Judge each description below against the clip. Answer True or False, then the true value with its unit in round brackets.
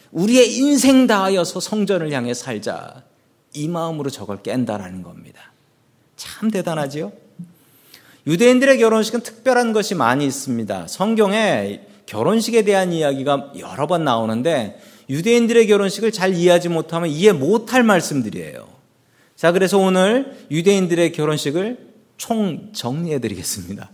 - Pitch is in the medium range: True (175 Hz)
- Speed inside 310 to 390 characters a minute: True (320 characters per minute)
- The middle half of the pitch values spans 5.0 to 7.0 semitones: False (7.4 semitones)